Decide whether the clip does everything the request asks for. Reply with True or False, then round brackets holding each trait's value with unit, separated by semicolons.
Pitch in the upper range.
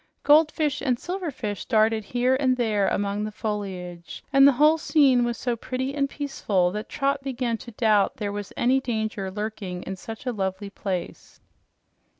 True (225 Hz)